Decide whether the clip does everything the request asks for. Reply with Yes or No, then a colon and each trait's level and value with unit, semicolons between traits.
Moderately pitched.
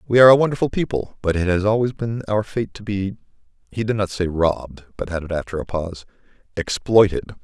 No: low, 100 Hz